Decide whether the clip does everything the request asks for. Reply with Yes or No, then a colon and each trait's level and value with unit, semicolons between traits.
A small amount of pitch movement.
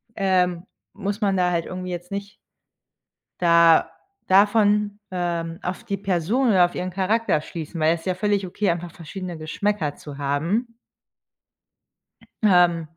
No: average, 3.2 semitones